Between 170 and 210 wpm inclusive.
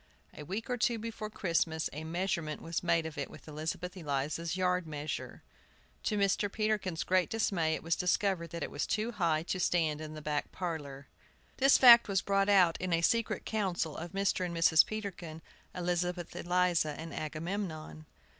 Yes: average, 175 wpm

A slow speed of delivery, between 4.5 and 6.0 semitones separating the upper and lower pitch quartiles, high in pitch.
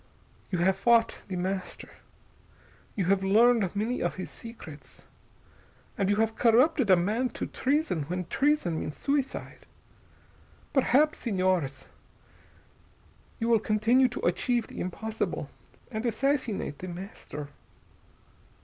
Yes: slow, 120 wpm; average, 4.9 semitones; high, 215 Hz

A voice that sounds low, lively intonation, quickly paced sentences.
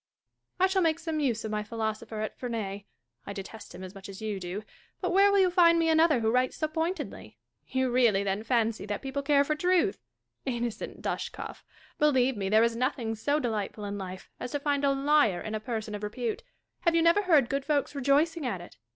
No: very high, 250 Hz; wide, 6.1 semitones; fast, 220 wpm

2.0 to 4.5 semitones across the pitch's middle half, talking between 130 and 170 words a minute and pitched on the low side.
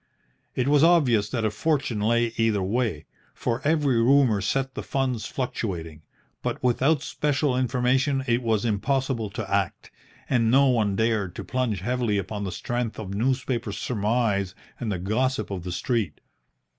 Yes: average, 4.1 semitones; average, 155 wpm; low, 120 Hz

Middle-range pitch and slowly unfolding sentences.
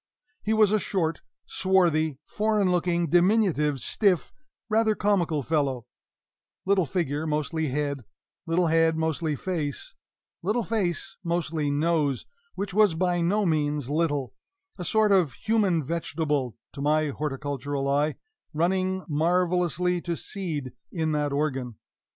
Yes: medium, 165 Hz; slow, 125 wpm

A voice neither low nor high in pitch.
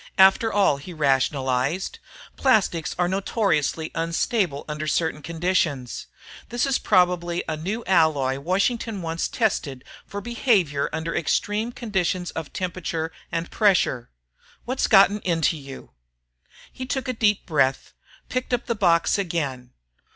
Yes: medium, 175 Hz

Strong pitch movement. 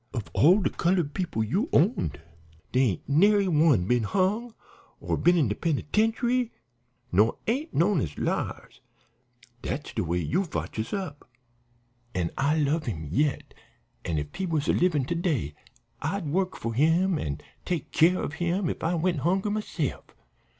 Yes: wide, 6.8 semitones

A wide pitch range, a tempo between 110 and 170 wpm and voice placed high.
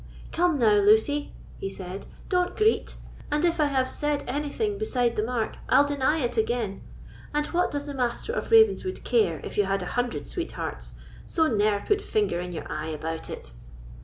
No: wide, 8.5 semitones; average, 185 wpm; very high, 270 Hz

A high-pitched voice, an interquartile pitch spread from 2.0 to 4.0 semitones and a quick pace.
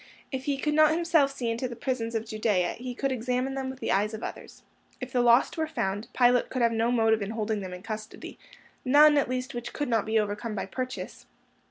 Yes: high, 240 Hz; average, 3.2 semitones; fast, 225 wpm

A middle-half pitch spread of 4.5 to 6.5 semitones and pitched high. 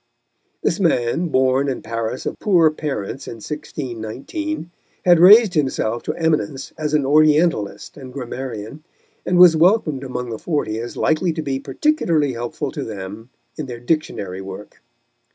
No: wide, 5.4 semitones; medium, 140 Hz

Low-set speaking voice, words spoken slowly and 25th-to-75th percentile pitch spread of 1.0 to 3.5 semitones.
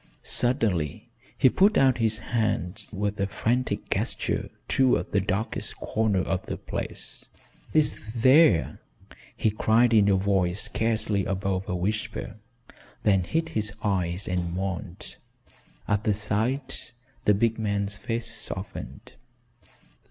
Yes: low, 105 Hz; slow, 125 wpm; average, 3.0 semitones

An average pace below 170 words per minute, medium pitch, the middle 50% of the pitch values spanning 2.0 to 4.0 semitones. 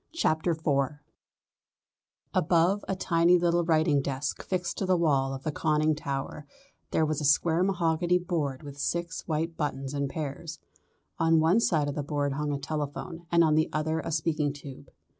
No: average, 175 wpm; medium, 155 Hz; average, 2.8 semitones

